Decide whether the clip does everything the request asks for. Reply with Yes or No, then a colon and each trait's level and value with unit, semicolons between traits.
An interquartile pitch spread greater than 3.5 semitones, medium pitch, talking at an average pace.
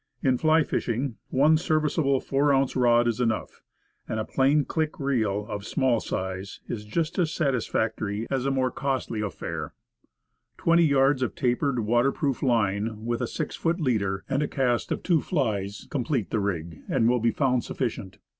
No: average, 4.3 semitones; low, 125 Hz; average, 175 wpm